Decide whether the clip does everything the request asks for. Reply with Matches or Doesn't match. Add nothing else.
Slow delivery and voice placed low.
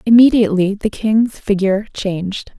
Doesn't match